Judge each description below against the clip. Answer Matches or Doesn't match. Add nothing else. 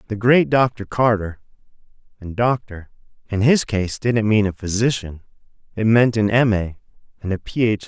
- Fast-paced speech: Doesn't match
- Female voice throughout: Doesn't match